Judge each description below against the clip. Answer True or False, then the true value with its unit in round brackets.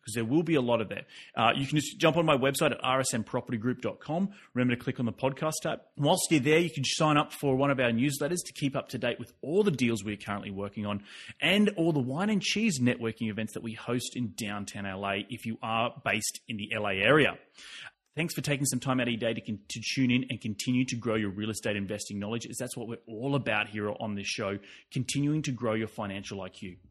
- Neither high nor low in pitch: False (120 Hz)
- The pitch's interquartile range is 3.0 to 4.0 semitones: False (4.5 semitones)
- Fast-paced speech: True (250 wpm)